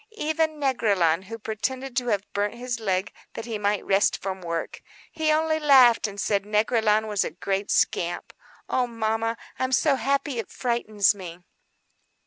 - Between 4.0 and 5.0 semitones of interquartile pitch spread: Yes, average, 4.4 semitones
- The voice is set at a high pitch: Yes, high, 220 Hz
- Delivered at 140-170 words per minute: Yes, average, 155 wpm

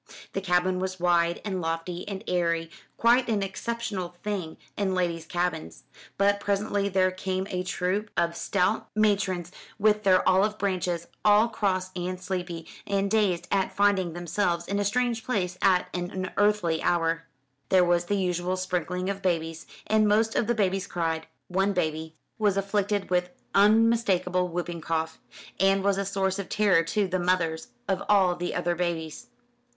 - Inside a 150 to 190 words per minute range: Yes, average, 160 wpm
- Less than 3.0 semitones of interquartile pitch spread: Yes, narrow, 2.5 semitones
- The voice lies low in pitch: No, medium, 185 Hz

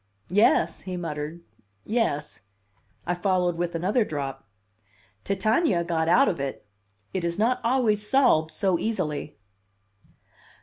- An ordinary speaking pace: No, slow, 120 wpm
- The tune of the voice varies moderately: Yes, average, 4.7 semitones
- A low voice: No, medium, 180 Hz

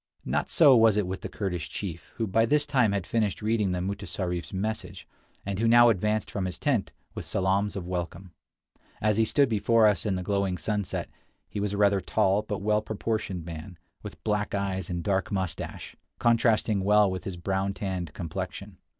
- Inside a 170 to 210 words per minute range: Yes, average, 190 wpm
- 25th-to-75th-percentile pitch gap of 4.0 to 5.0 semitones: No, narrow, 2.6 semitones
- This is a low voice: Yes, low, 100 Hz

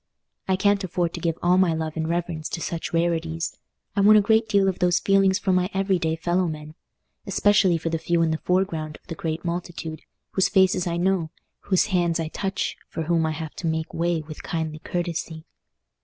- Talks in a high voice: No, medium, 170 Hz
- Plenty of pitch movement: No, narrow, 2.6 semitones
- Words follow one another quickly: Yes, fast, 210 wpm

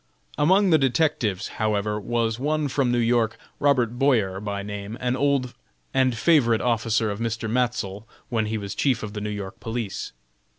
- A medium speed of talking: Yes, average, 170 wpm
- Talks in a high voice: No, low, 115 Hz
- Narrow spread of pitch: No, average, 3.5 semitones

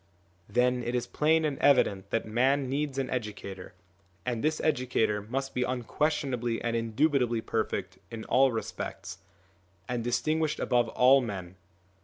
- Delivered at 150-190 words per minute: No, average, 140 wpm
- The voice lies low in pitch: Yes, low, 125 Hz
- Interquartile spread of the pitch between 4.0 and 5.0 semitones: No, average, 3.2 semitones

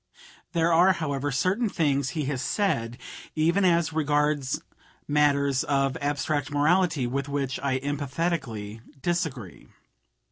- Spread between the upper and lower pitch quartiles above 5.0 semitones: No, average, 3.3 semitones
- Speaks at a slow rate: Yes, slow, 115 wpm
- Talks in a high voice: No, medium, 145 Hz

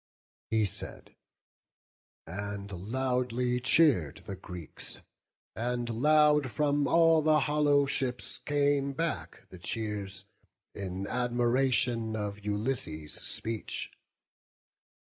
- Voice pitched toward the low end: Yes, low, 120 Hz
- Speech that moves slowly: Yes, slow, 90 wpm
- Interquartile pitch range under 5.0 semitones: No, wide, 5.6 semitones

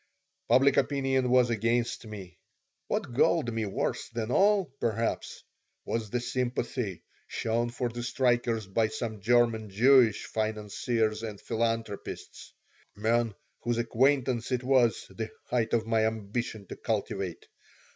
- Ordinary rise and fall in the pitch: No, narrow, 2.0 semitones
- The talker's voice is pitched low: Yes, low, 115 Hz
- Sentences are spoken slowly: Yes, slow, 125 wpm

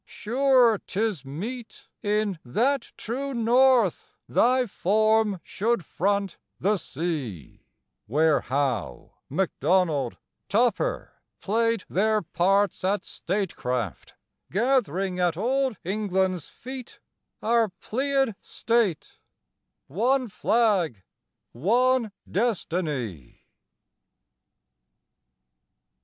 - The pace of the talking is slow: Yes, slow, 80 wpm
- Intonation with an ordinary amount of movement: No, wide, 5.7 semitones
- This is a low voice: No, high, 205 Hz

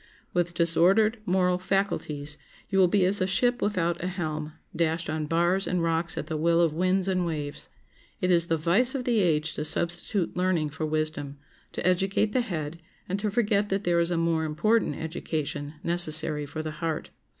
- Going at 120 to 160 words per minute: No, average, 190 wpm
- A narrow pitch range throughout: No, average, 3.2 semitones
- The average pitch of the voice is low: No, medium, 170 Hz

